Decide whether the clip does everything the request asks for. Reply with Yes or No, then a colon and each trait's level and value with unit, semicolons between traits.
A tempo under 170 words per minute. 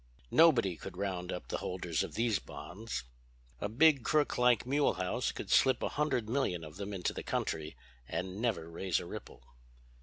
No: average, 175 wpm